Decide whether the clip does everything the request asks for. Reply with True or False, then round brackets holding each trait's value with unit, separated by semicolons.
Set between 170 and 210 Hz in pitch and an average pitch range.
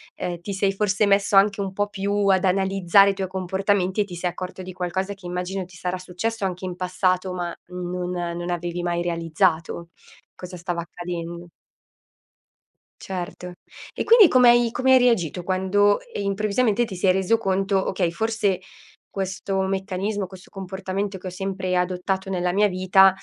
False (190 Hz; 1.8 semitones)